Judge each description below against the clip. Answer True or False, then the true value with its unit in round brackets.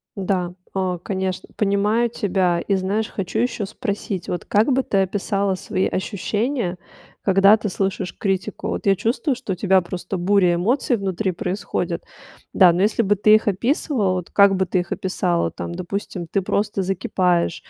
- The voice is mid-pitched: False (195 Hz)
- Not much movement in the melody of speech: True (2.3 semitones)